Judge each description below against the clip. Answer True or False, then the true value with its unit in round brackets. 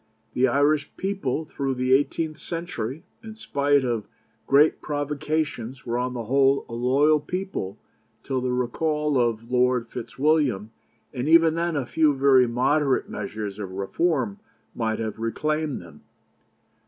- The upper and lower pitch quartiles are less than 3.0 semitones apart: False (4.1 semitones)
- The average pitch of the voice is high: False (135 Hz)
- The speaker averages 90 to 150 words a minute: True (140 wpm)